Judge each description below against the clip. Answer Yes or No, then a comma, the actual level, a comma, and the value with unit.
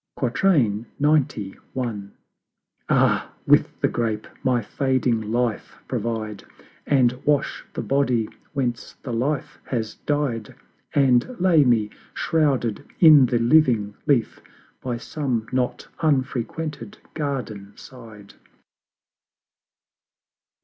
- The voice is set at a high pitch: No, low, 125 Hz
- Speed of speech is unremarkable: No, slow, 95 wpm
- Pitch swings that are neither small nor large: Yes, average, 3.9 semitones